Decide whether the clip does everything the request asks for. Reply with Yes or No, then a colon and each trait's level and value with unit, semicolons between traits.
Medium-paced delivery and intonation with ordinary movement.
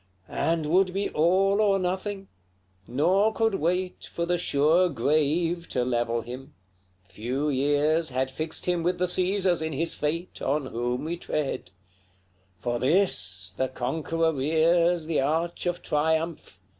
Yes: average, 145 wpm; average, 4.5 semitones